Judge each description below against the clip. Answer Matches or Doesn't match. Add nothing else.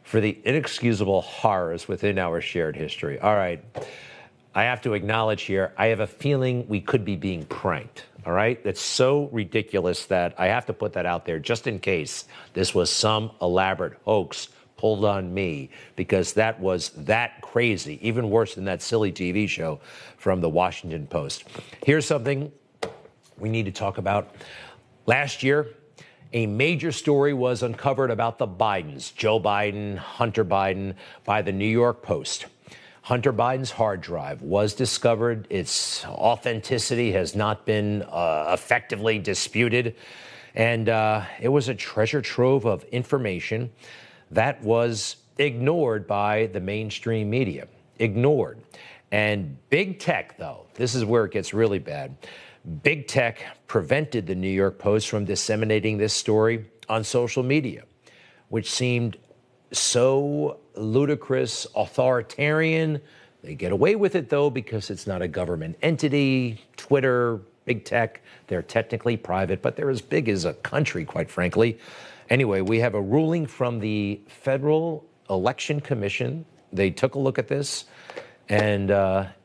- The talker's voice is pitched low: Matches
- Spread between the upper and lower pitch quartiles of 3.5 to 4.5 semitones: Matches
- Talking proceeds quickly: Doesn't match